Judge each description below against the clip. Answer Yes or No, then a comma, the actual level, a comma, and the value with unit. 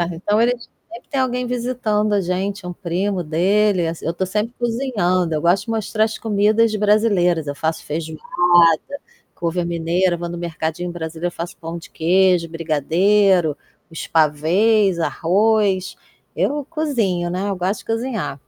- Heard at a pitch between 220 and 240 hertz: No, medium, 185 Hz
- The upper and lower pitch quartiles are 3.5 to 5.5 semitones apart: Yes, average, 4.1 semitones